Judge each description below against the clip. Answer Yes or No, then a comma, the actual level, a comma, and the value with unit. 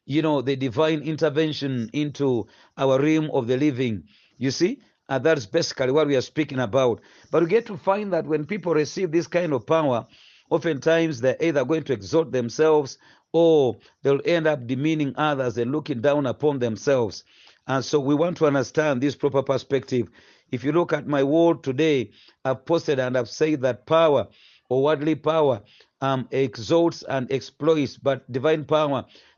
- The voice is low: No, medium, 150 Hz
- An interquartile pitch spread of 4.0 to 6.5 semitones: No, average, 3.1 semitones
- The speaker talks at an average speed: Yes, average, 175 wpm